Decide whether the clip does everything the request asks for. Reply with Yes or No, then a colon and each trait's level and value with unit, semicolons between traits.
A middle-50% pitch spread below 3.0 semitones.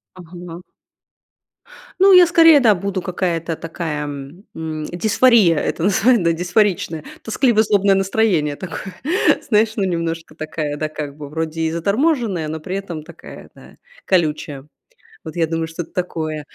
No: average, 4.1 semitones